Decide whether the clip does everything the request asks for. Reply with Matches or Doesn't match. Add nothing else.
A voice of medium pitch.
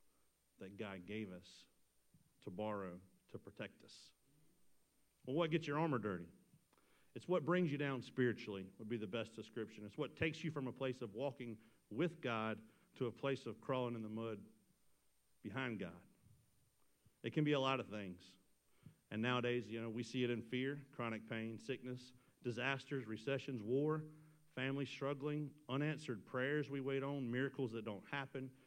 Doesn't match